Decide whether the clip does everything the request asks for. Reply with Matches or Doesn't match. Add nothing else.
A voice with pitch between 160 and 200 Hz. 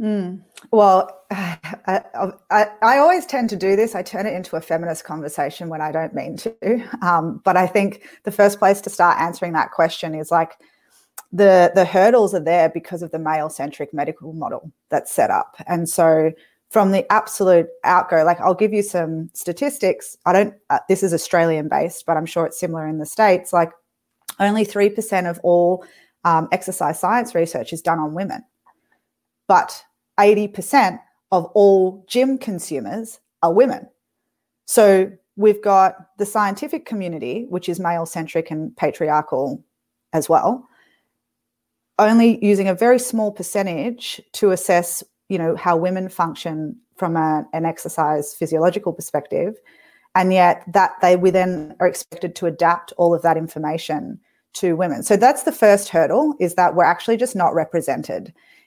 Matches